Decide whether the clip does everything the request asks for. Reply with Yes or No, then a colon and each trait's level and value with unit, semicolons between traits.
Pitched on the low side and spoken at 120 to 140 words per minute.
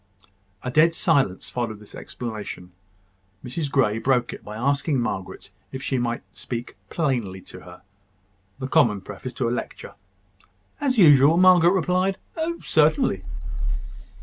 Yes: low, 130 Hz; slow, 135 wpm